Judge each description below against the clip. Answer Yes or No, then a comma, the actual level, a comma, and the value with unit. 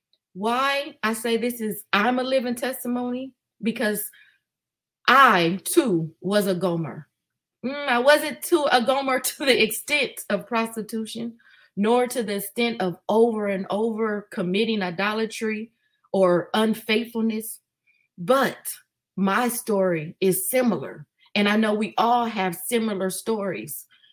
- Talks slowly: Yes, slow, 125 wpm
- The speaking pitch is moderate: No, high, 220 Hz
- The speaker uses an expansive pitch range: No, average, 4.0 semitones